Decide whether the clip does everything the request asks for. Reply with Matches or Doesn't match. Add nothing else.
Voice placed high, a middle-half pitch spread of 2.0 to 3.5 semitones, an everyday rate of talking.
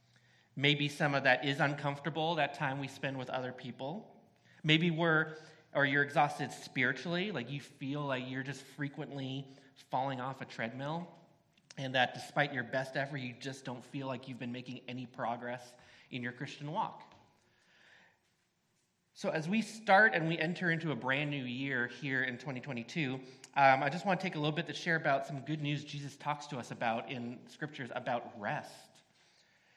Doesn't match